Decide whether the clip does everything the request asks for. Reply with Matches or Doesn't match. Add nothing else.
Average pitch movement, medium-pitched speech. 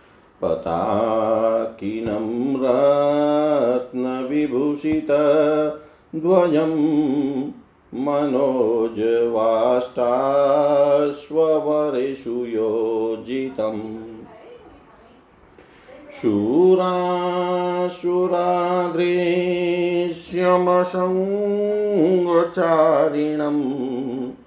Doesn't match